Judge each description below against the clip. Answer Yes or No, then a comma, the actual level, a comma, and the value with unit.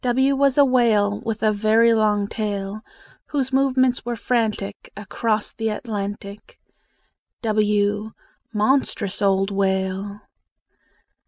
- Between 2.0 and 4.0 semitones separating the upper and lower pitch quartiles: Yes, average, 2.9 semitones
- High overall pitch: Yes, high, 215 Hz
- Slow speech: Yes, slow, 105 wpm